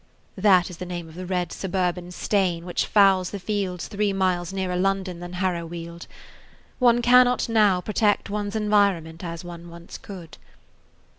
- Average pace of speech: Yes, average, 155 wpm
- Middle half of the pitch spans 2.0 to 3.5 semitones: Yes, narrow, 2.6 semitones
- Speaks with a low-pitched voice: No, medium, 185 Hz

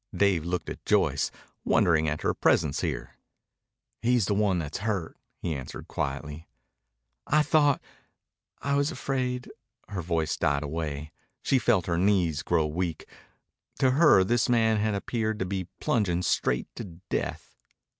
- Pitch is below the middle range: Yes, very low, 95 Hz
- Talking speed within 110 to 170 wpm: Yes, average, 150 wpm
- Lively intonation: Yes, wide, 6.5 semitones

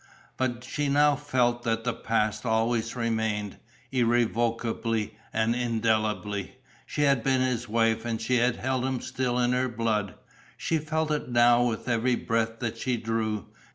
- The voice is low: Yes, low, 120 Hz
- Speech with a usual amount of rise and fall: No, narrow, 2.1 semitones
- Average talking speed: Yes, average, 155 wpm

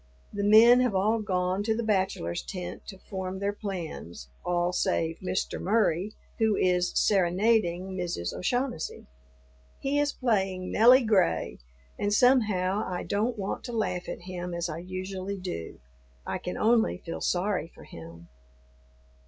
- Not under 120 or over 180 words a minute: Yes, average, 145 wpm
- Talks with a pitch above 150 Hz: Yes, high, 190 Hz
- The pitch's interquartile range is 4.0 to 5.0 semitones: No, average, 3.4 semitones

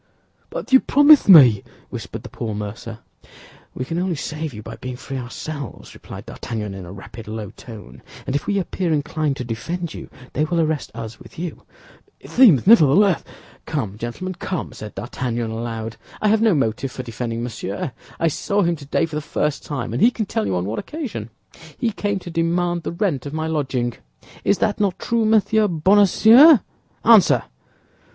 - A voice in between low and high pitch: Yes, medium, 150 Hz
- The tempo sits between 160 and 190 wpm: Yes, average, 185 wpm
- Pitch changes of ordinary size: No, wide, 8.4 semitones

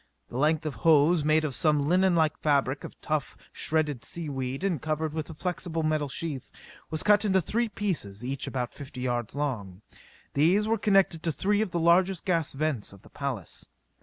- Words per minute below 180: No, average, 190 wpm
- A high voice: No, medium, 155 Hz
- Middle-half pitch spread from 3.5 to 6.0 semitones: Yes, average, 4.1 semitones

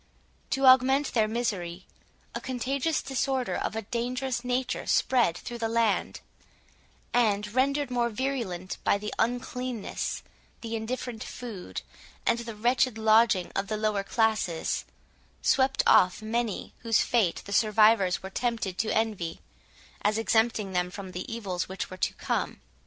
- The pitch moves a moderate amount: Yes, average, 3.5 semitones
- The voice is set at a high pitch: Yes, high, 225 Hz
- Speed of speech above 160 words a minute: No, average, 140 wpm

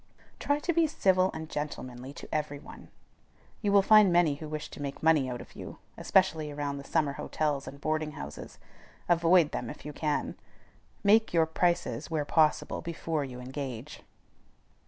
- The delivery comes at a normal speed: Yes, average, 170 wpm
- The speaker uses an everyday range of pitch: Yes, average, 3.5 semitones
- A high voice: No, medium, 155 Hz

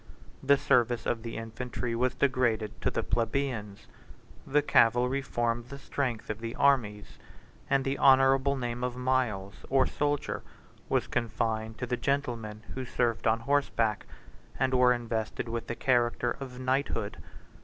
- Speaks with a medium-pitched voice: No, low, 120 Hz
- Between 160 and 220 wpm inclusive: No, average, 150 wpm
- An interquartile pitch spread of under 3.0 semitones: Yes, narrow, 2.5 semitones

